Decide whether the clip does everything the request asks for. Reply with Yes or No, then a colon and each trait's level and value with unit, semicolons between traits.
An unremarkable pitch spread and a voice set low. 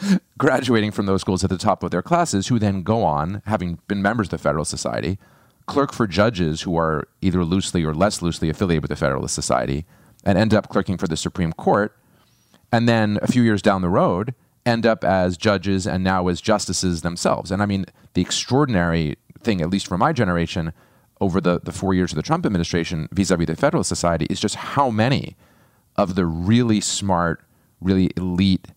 Yes: average, 3.4 semitones; very low, 95 Hz